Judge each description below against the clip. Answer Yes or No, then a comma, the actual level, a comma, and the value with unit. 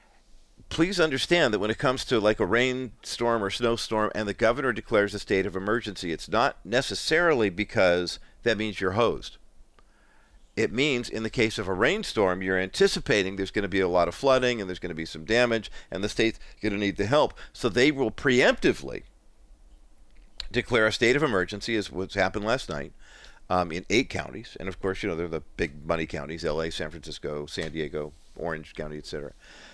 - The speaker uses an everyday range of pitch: Yes, average, 5.0 semitones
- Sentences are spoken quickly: No, average, 195 wpm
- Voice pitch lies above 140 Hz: No, low, 100 Hz